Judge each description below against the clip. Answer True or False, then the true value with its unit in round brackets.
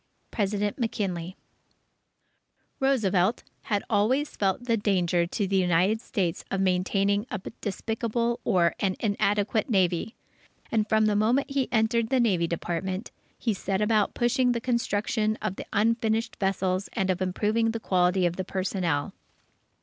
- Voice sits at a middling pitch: False (205 Hz)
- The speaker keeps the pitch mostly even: False (3.3 semitones)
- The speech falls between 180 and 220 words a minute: False (145 wpm)